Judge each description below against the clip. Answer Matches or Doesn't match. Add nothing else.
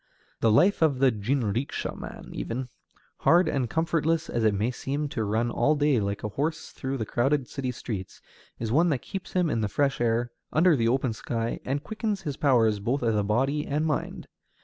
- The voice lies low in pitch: Matches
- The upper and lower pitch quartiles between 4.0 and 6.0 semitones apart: Matches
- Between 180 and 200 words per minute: Matches